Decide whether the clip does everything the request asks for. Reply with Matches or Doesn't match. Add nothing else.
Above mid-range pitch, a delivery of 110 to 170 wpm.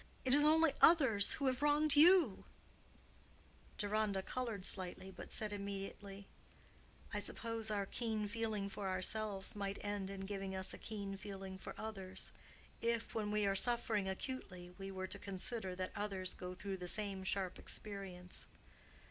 Matches